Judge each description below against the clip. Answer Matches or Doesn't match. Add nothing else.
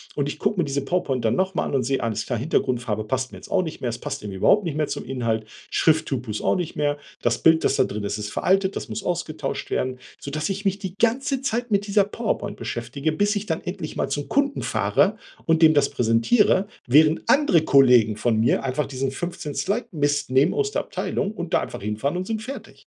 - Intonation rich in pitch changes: Matches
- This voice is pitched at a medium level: Matches